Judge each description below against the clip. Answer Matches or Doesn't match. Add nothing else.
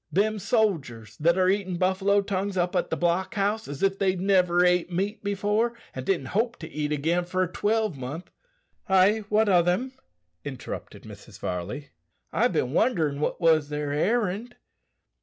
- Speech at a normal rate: Matches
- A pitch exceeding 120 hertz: Matches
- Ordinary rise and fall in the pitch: Matches